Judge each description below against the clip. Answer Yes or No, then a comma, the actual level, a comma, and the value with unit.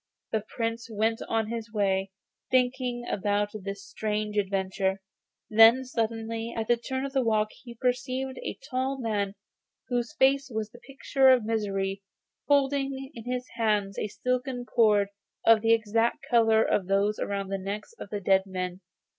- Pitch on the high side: Yes, high, 225 Hz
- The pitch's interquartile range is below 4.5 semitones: Yes, average, 3.5 semitones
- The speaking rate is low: No, average, 160 wpm